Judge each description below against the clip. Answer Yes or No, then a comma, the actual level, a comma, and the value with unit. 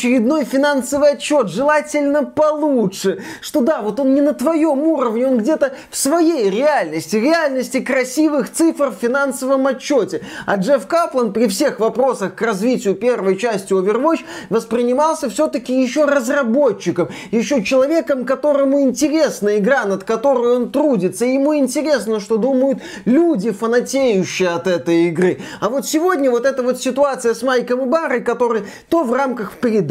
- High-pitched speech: Yes, very high, 260 Hz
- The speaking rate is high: No, average, 145 wpm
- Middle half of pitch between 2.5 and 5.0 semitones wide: Yes, average, 4.2 semitones